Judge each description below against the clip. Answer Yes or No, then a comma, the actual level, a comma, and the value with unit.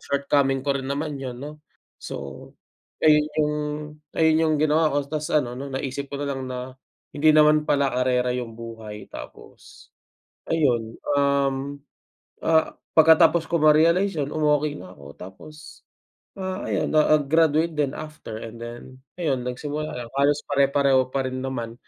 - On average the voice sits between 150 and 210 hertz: No, medium, 140 Hz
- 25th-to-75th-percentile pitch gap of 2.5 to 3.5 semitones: Yes, average, 3.1 semitones